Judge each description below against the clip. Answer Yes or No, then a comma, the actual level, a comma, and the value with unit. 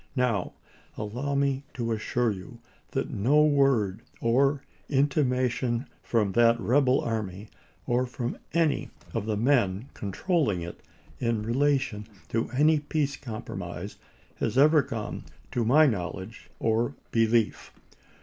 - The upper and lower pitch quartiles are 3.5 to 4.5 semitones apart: Yes, average, 4.2 semitones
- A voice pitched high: No, low, 120 Hz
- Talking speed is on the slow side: Yes, slow, 120 wpm